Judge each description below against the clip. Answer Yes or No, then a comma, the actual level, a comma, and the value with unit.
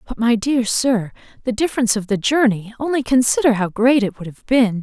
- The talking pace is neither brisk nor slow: No, fast, 210 wpm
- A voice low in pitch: No, high, 235 Hz